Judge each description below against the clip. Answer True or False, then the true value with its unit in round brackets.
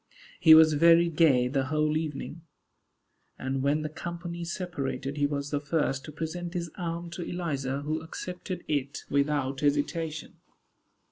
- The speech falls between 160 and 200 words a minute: False (145 wpm)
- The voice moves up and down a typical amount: True (3.1 semitones)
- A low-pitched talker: False (155 Hz)